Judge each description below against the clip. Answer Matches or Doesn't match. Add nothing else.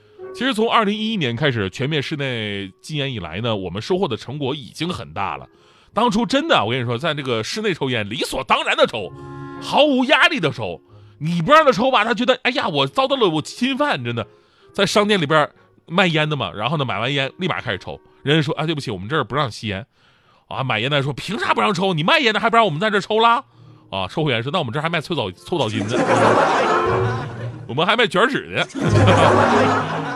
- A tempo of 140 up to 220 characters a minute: Doesn't match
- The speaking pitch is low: Doesn't match